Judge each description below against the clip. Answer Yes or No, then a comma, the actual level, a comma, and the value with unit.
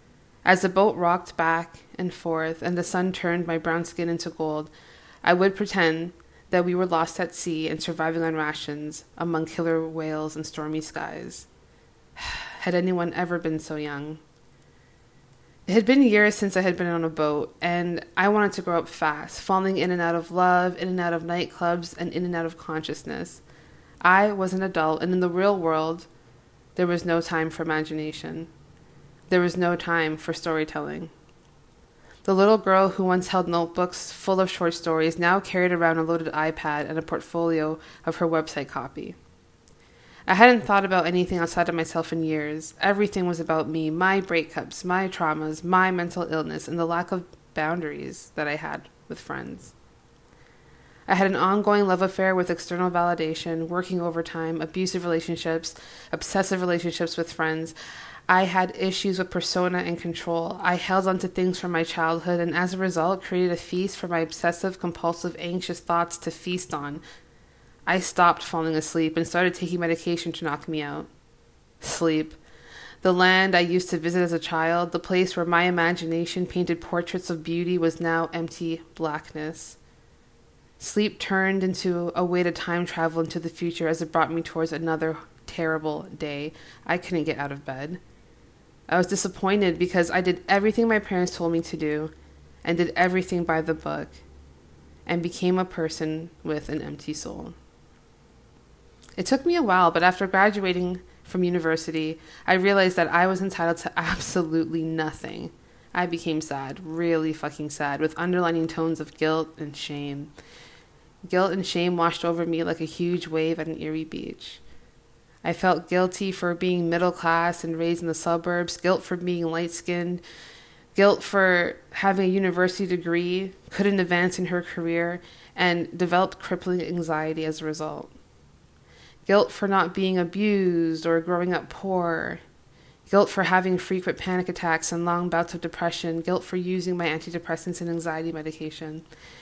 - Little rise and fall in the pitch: Yes, narrow, 2.0 semitones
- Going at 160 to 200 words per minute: Yes, average, 170 wpm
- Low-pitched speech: No, medium, 170 Hz